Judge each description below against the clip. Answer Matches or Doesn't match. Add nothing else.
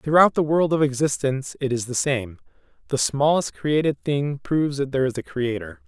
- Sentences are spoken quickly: Doesn't match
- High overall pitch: Doesn't match